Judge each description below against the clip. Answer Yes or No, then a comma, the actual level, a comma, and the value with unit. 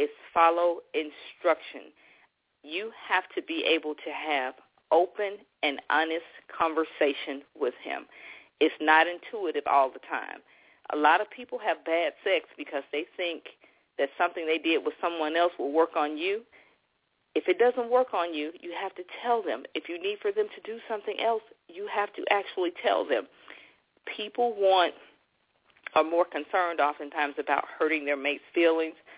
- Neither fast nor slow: Yes, average, 165 wpm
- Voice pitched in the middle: Yes, medium, 175 Hz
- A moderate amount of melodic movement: No, wide, 7.4 semitones